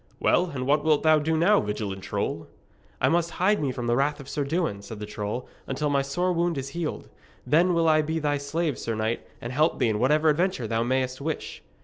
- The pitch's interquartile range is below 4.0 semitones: No, average, 4.4 semitones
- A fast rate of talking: Yes, fast, 230 wpm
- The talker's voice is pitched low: No, medium, 145 Hz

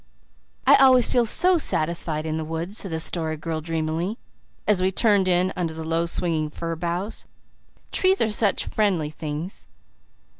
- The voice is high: No, medium, 170 Hz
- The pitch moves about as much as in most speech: Yes, average, 4.1 semitones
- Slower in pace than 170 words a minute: Yes, average, 160 wpm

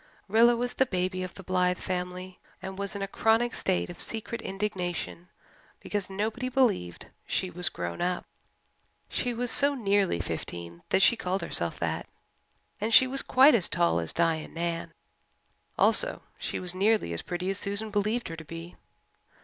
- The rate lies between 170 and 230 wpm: Yes, average, 175 wpm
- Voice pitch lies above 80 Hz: Yes, high, 190 Hz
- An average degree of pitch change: Yes, average, 4.1 semitones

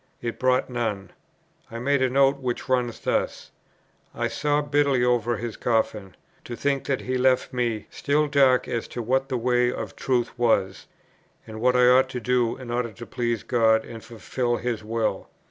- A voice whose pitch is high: No, low, 125 Hz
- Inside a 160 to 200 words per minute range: Yes, average, 180 wpm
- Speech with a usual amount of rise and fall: No, narrow, 1.9 semitones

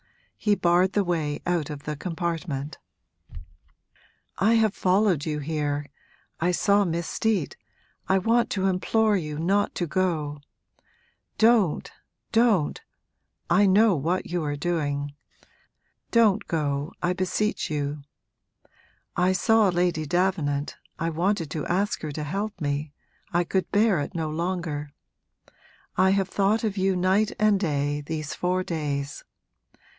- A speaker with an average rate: No, slow, 130 wpm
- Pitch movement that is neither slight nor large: Yes, average, 4.5 semitones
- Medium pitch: Yes, medium, 175 Hz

